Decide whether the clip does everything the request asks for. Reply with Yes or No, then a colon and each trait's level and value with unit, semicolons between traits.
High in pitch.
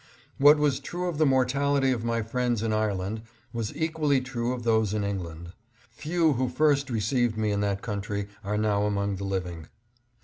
No: low, 115 Hz